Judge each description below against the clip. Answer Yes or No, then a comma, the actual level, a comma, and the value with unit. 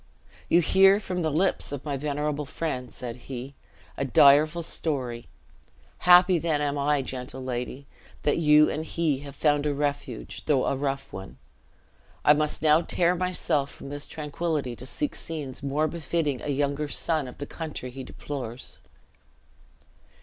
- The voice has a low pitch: No, medium, 145 Hz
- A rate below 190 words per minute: Yes, average, 155 wpm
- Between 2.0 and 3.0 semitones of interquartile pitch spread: Yes, average, 2.7 semitones